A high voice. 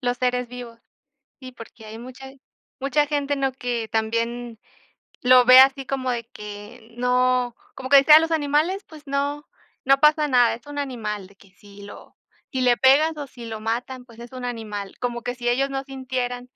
Yes: very high, 250 Hz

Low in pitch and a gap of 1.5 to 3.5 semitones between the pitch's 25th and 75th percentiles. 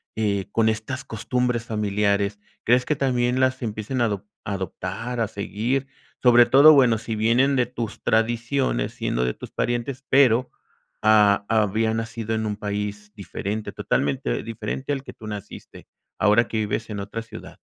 Yes: low, 110 Hz; average, 2.9 semitones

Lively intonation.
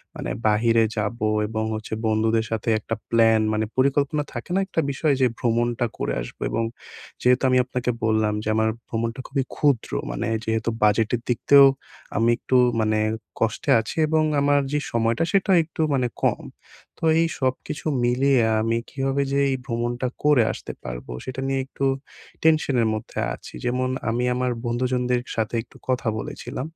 No: average, 3.2 semitones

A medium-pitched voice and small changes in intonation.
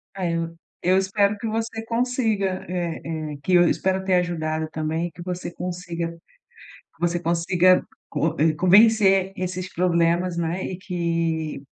Yes: medium, 175 Hz; narrow, 2.2 semitones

